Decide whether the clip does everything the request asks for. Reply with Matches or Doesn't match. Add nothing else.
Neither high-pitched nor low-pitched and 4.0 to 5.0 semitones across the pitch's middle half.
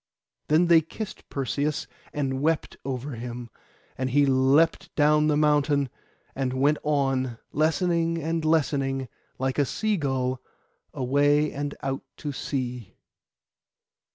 Doesn't match